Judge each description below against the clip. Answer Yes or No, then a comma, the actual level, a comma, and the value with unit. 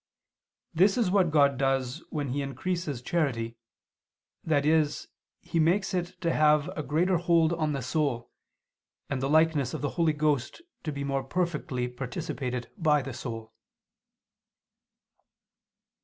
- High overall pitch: No, medium, 150 Hz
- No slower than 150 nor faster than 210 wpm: No, average, 140 wpm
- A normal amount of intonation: Yes, average, 3.8 semitones